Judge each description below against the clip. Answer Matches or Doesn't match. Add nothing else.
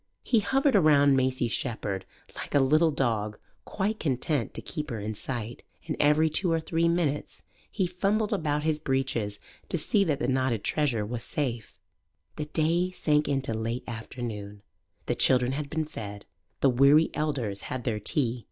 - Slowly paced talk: Doesn't match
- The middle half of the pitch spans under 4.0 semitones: Doesn't match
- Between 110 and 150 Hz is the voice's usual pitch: Matches